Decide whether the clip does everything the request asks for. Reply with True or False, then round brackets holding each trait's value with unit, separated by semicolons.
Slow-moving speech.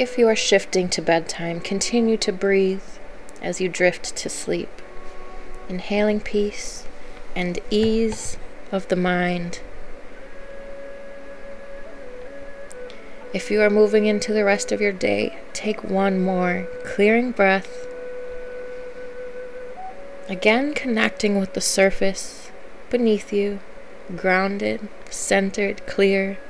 True (105 wpm)